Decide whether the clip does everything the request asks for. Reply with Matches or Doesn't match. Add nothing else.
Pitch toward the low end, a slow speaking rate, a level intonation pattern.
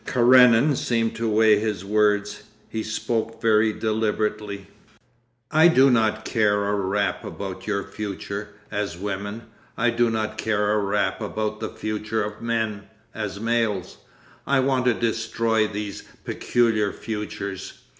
Matches